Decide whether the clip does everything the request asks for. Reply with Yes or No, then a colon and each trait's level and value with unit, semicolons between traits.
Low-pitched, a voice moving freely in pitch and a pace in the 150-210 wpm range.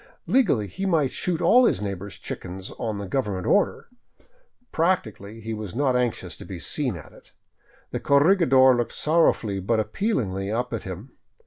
Yes: low, 115 Hz; wide, 7.1 semitones; average, 155 wpm